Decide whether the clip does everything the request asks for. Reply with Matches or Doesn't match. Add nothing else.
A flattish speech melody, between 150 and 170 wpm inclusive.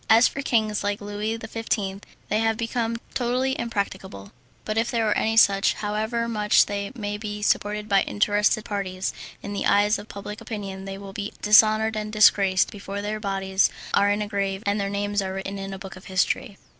Doesn't match